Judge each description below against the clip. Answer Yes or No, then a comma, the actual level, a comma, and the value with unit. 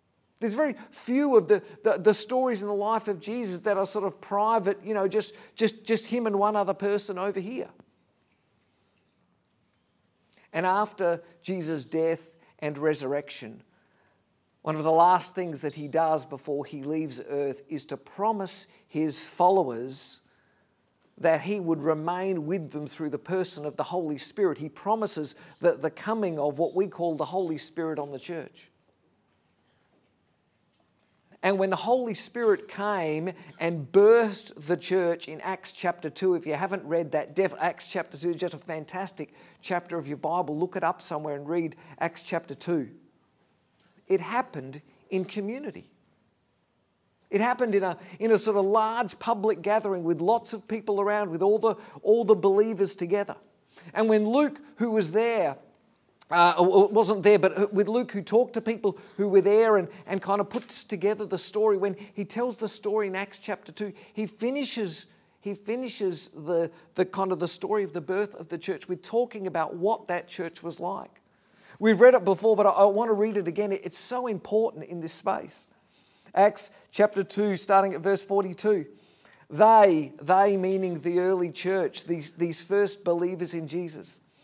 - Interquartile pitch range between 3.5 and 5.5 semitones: Yes, average, 3.9 semitones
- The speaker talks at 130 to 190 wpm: Yes, average, 175 wpm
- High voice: Yes, high, 195 Hz